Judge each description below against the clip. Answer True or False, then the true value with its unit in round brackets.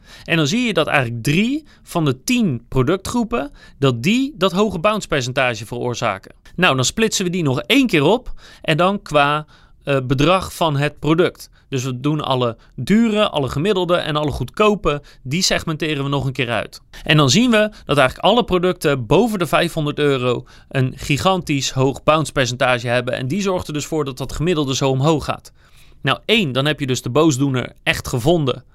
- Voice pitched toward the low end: False (150 Hz)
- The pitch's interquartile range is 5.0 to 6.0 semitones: True (5.4 semitones)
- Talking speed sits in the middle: True (190 wpm)